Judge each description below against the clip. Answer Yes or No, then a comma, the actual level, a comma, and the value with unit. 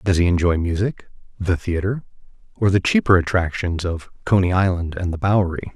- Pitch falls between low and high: No, very low, 90 Hz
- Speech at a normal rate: Yes, average, 165 wpm